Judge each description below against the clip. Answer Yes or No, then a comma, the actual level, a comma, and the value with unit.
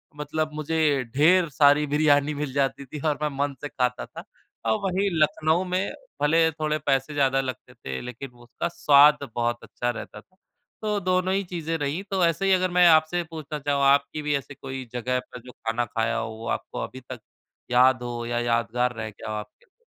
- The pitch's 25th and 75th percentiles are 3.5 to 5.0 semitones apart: Yes, average, 4.2 semitones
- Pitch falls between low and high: Yes, medium, 145 Hz